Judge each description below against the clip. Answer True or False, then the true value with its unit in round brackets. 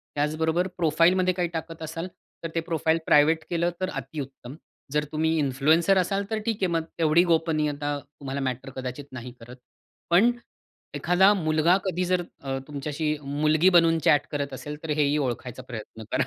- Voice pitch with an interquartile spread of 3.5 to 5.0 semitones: False (3.1 semitones)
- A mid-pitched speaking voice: True (155 Hz)